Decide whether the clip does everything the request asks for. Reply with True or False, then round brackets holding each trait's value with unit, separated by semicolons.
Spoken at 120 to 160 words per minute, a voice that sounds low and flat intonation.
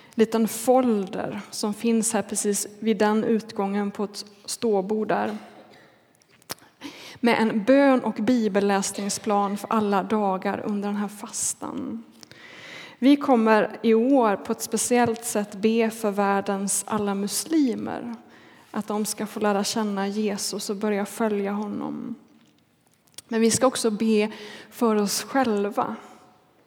False (130 wpm; 215 Hz; 2.0 semitones)